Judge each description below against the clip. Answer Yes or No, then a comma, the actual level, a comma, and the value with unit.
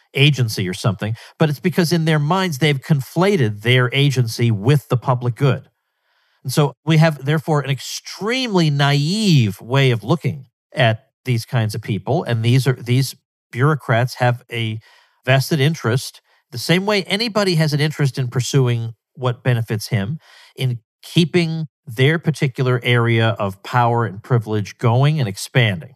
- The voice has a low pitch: Yes, low, 130 Hz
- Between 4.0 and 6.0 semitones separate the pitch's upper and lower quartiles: Yes, average, 4.6 semitones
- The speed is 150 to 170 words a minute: Yes, average, 155 wpm